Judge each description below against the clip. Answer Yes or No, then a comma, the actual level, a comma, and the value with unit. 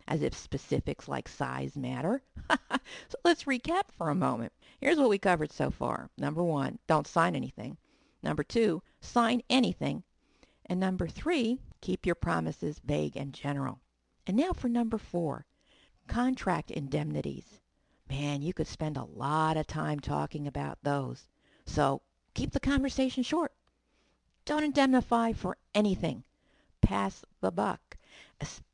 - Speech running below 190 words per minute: Yes, average, 140 wpm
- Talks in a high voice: No, medium, 175 Hz